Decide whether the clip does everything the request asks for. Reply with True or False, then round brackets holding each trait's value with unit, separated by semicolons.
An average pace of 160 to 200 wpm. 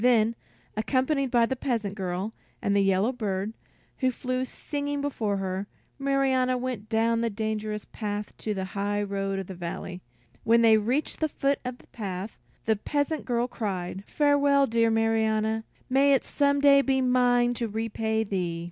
True (165 wpm)